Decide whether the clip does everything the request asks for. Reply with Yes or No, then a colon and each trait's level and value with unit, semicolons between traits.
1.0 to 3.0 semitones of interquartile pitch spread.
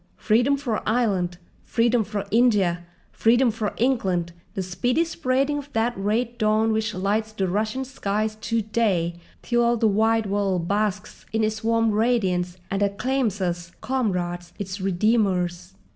No: average, 3.6 semitones